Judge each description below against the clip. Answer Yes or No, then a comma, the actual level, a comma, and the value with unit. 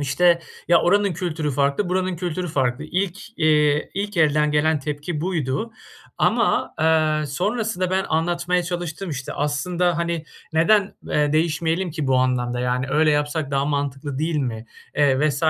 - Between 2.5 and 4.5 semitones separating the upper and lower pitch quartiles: Yes, average, 3.5 semitones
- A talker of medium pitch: Yes, medium, 155 Hz